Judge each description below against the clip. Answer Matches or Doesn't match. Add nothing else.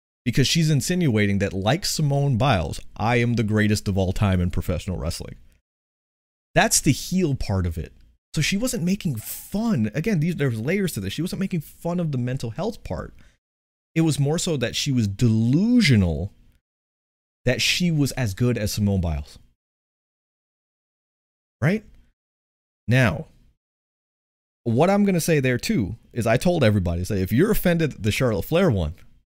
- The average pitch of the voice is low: Matches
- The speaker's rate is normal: Matches